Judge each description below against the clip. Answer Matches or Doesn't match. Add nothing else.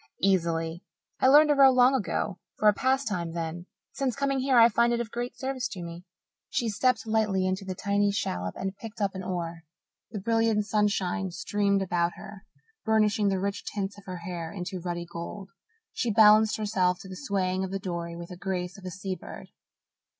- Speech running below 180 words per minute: Doesn't match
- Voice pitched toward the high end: Matches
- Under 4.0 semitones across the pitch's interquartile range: Matches